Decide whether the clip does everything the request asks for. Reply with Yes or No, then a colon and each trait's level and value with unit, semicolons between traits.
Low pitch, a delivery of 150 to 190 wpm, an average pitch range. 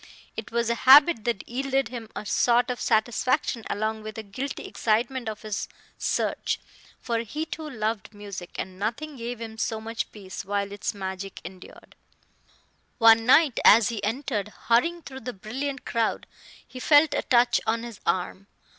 No: high, 230 Hz; average, 165 wpm; average, 3.4 semitones